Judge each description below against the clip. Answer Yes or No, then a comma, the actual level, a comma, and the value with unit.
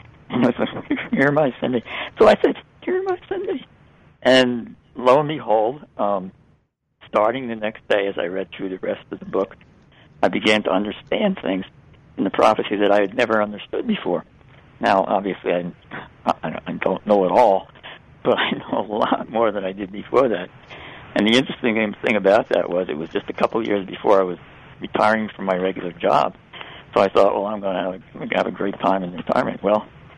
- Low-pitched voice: Yes, low, 105 Hz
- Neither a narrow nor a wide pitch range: Yes, average, 4.1 semitones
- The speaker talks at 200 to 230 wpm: Yes, fast, 205 wpm